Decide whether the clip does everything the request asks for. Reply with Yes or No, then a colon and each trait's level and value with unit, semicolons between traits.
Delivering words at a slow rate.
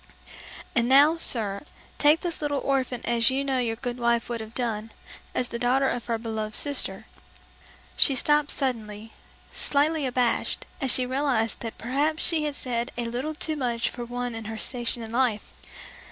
No: average, 175 wpm